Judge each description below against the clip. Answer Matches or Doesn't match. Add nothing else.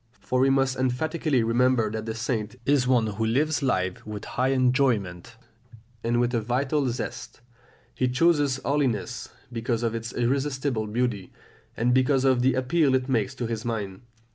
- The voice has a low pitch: Matches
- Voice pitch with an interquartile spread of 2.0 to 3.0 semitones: Matches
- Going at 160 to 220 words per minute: Matches